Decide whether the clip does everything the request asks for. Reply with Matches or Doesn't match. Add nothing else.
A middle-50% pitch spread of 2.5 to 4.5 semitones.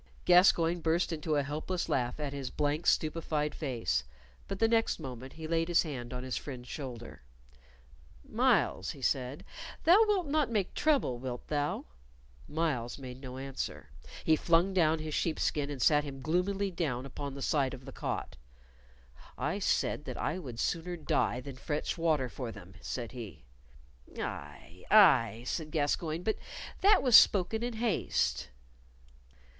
Doesn't match